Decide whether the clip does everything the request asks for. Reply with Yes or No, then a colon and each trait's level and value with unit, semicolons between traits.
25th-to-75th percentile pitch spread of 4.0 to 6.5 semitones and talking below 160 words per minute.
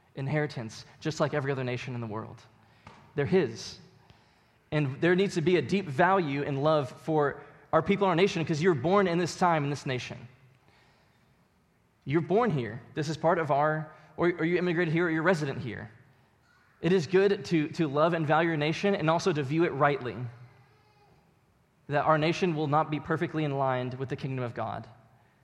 No: average, 4.5 semitones; average, 195 wpm